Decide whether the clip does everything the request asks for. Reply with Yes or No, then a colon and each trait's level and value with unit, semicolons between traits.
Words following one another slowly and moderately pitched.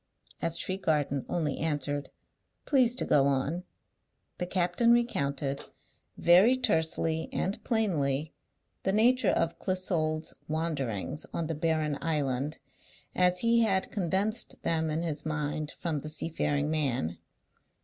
Yes: slow, 120 wpm; medium, 160 Hz